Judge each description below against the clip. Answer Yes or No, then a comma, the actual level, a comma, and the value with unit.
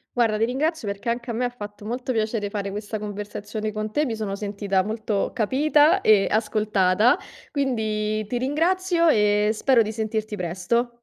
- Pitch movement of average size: Yes, average, 3.0 semitones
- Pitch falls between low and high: No, high, 215 Hz